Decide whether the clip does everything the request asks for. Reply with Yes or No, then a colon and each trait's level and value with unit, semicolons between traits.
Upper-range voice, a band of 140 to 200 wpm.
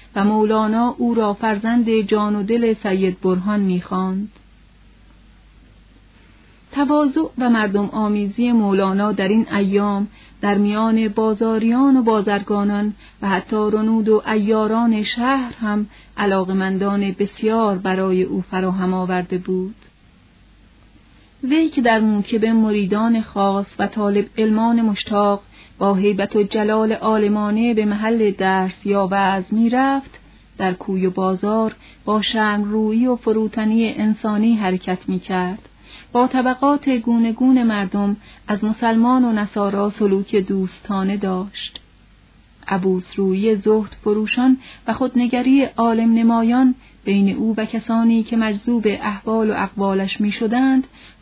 No: high, 210 Hz; average, 120 wpm